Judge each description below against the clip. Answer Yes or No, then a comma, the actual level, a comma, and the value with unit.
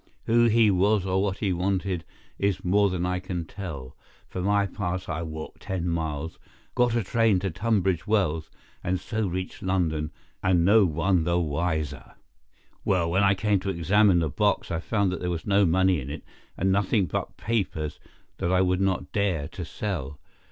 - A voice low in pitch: Yes, very low, 95 Hz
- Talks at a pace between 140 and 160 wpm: No, average, 180 wpm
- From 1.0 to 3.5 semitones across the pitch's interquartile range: Yes, average, 3.0 semitones